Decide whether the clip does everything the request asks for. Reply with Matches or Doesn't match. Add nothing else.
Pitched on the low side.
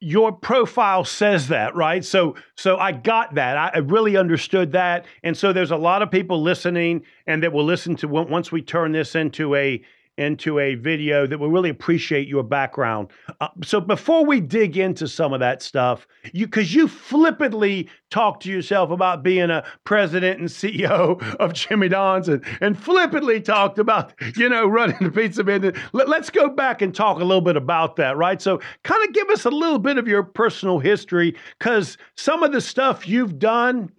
Doesn't match